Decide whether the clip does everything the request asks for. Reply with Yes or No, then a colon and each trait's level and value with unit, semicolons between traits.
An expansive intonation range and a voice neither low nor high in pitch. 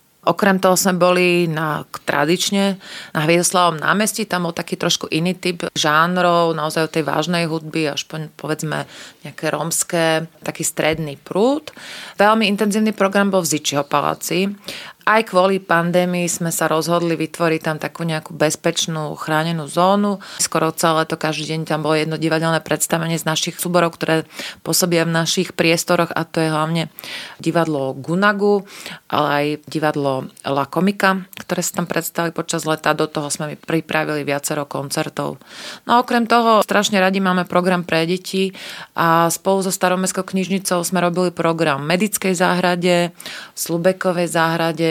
No: average, 2.8 semitones; medium, 170 Hz